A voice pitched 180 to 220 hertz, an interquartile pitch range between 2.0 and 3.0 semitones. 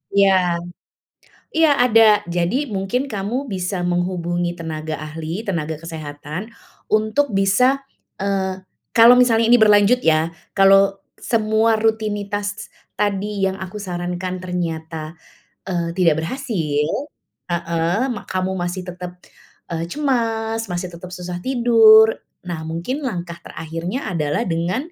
No: high, 190 Hz; average, 4.3 semitones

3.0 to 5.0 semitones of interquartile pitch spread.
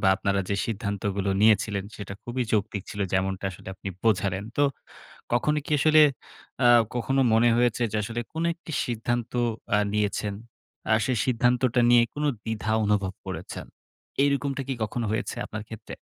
Yes: average, 3.5 semitones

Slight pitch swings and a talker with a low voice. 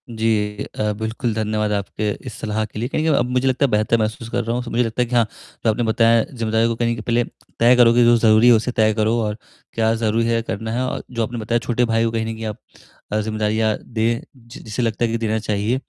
Yes: narrow, 1.4 semitones; low, 115 Hz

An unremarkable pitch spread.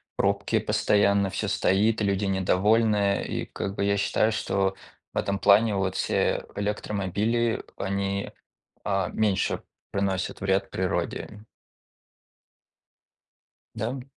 No: narrow, 1.5 semitones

